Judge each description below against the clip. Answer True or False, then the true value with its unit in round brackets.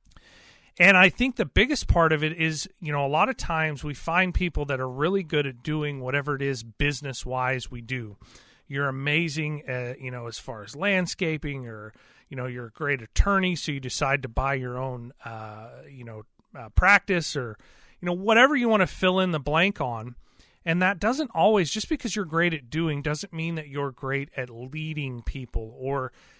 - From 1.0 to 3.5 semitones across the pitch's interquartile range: False (5.2 semitones)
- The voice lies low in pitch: False (145 Hz)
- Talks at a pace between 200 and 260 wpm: True (205 wpm)